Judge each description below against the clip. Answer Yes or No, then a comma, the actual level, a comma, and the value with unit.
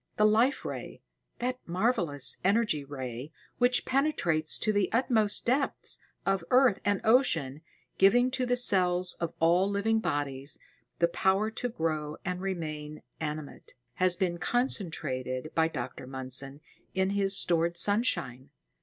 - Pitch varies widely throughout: Yes, wide, 6.5 semitones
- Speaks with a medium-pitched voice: Yes, medium, 180 Hz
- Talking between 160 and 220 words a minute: No, slow, 135 wpm